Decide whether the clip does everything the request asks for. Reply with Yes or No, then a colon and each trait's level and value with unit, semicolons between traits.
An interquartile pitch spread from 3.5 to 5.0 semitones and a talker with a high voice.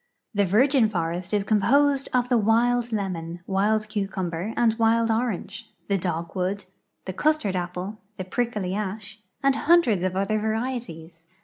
Yes: average, 3.8 semitones; high, 210 Hz